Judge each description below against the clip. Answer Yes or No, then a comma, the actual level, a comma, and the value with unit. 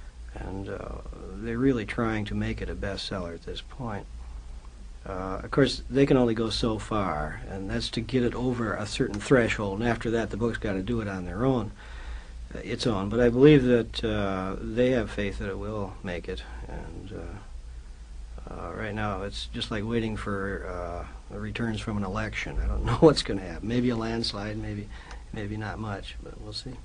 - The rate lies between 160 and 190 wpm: No, fast, 205 wpm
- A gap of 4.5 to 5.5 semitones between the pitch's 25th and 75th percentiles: No, average, 3.5 semitones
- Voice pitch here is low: Yes, low, 105 Hz